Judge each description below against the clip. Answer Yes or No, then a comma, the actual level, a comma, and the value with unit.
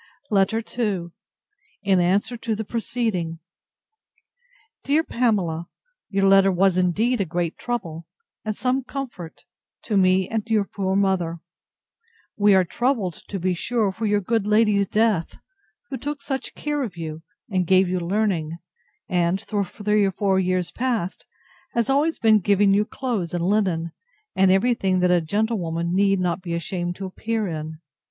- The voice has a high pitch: Yes, high, 195 Hz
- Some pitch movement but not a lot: Yes, average, 3.8 semitones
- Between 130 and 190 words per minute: Yes, average, 160 wpm